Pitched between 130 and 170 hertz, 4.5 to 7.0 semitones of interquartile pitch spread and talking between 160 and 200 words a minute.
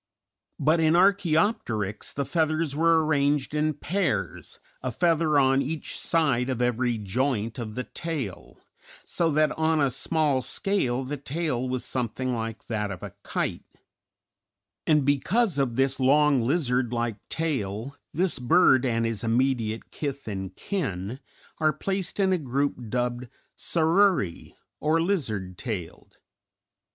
No: low, 135 Hz; average, 5.1 semitones; slow, 135 wpm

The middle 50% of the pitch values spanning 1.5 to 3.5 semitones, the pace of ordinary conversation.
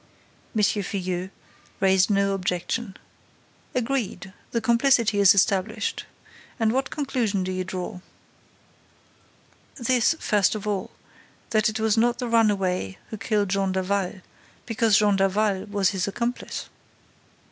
No: average, 3.0 semitones; slow, 125 wpm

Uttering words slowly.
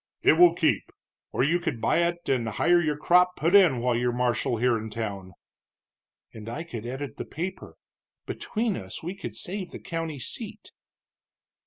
No: average, 175 wpm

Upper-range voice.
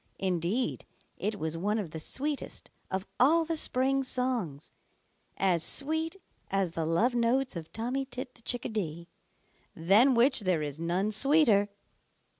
Yes: high, 220 Hz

